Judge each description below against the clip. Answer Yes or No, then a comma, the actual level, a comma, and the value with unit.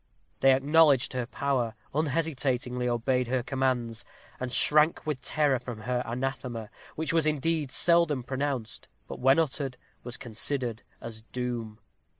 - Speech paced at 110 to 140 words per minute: Yes, slow, 135 wpm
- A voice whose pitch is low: Yes, low, 130 Hz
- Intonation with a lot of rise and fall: No, average, 3.1 semitones